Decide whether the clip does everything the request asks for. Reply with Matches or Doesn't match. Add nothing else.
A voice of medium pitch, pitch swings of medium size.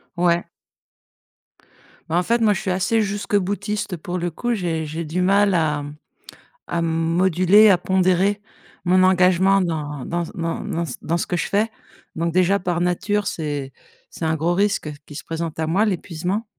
Matches